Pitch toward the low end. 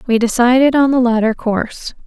No: high, 240 Hz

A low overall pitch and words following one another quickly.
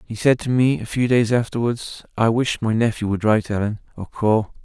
Yes: low, 115 Hz; fast, 220 wpm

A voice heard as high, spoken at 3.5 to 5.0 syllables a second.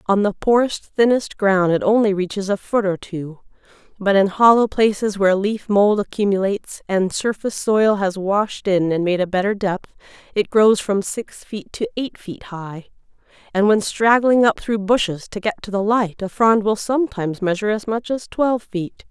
Yes: high, 205 Hz; 4.9 syllables/s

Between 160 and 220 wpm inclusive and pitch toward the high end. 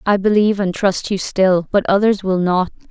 Yes: fast, 205 wpm; high, 195 Hz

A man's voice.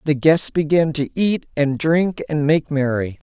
Yes: male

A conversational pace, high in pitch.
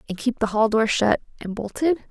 No: fast, 230 wpm; high, 230 Hz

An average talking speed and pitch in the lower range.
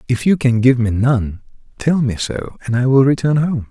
No: fast, 225 wpm; low, 125 Hz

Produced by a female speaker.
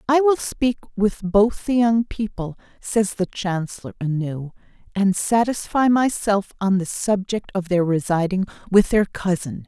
Yes: female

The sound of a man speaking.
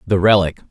Yes: male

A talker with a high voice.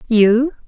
Yes: high, 240 Hz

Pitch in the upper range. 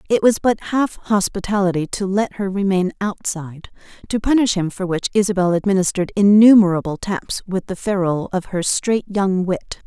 Yes: high, 195 Hz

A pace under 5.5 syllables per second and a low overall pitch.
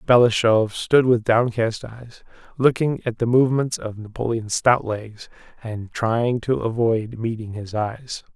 Yes: 4.0 syllables/s; low, 115 Hz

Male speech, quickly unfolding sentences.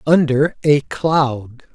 No: male; slow, 105 wpm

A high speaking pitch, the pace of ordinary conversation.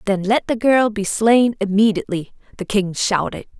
Yes: high, 210 Hz; average, 165 wpm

